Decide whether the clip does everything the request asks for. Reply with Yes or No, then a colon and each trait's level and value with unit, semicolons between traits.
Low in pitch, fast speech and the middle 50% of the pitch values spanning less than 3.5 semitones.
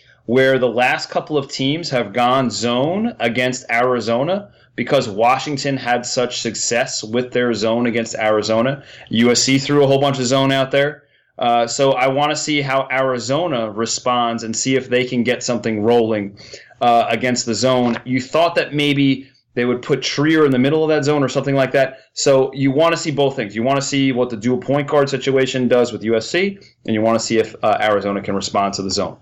Yes: low, 125 Hz; fast, 210 wpm; average, 2.9 semitones